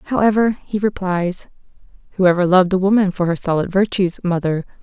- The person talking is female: Yes, female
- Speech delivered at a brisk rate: No, average, 160 wpm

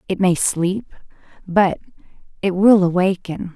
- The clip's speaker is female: Yes, female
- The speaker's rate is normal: No, slow, 120 wpm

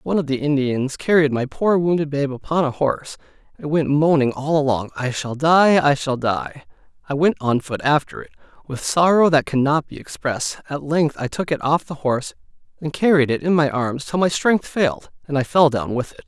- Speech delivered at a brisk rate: Yes, fast, 215 wpm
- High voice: No, medium, 145 Hz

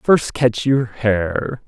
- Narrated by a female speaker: No, male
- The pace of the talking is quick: No, average, 145 wpm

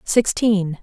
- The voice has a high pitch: Yes, high, 200 Hz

